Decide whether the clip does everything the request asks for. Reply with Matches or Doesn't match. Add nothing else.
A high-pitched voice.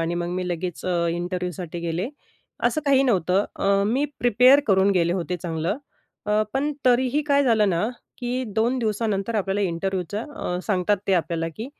Matches